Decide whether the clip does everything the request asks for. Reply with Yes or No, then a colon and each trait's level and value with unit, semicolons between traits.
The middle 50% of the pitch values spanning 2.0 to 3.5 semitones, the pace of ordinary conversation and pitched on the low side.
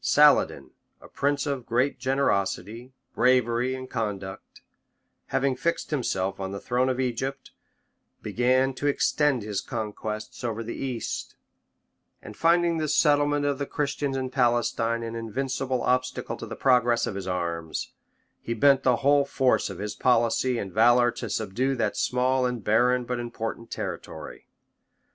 Yes: average, 2.8 semitones; average, 150 wpm; low, 125 Hz